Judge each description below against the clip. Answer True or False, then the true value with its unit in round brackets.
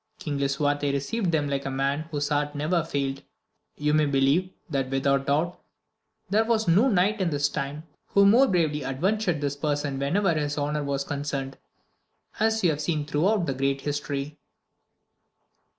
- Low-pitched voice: False (145 Hz)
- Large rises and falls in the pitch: False (3.7 semitones)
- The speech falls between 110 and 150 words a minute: False (165 wpm)